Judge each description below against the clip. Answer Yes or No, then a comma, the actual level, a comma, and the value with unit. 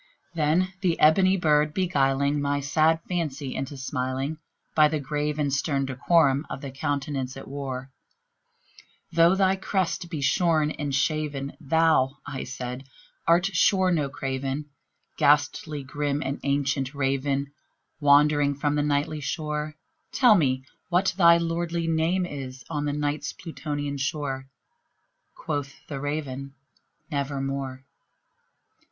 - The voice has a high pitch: No, medium, 145 Hz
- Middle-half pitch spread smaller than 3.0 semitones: Yes, narrow, 2.6 semitones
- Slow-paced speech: Yes, slow, 125 wpm